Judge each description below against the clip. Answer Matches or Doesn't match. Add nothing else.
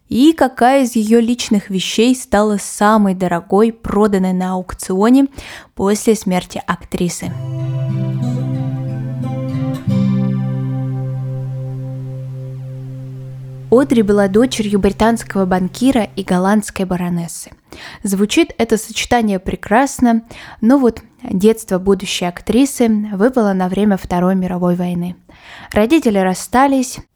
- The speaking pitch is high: Matches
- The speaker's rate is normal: Doesn't match